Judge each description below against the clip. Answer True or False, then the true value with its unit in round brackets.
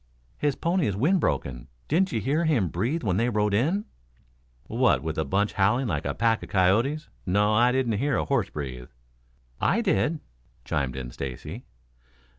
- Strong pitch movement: True (7.4 semitones)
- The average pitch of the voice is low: True (115 Hz)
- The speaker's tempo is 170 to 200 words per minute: True (175 wpm)